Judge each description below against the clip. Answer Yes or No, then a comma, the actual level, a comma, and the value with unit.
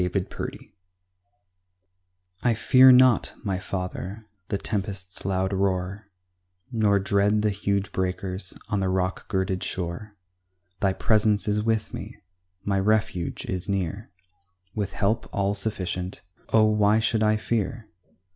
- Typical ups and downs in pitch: No, narrow, 2.3 semitones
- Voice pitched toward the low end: Yes, low, 100 Hz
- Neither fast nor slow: No, slow, 125 wpm